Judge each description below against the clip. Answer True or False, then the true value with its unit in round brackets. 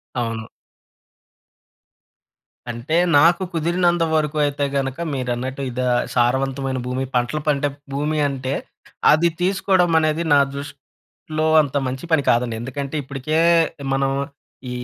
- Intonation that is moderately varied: True (3.4 semitones)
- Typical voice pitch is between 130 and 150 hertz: True (140 Hz)